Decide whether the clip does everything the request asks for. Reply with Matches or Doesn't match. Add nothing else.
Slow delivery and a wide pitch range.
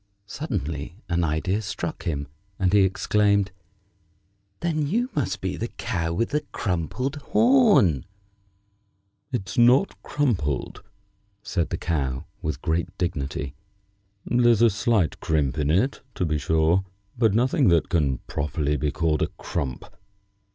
Matches